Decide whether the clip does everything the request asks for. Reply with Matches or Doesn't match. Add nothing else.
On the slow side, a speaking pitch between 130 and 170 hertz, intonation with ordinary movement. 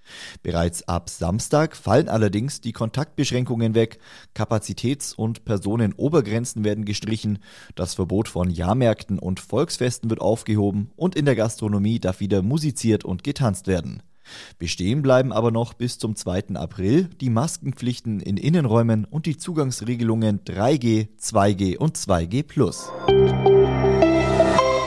Doesn't match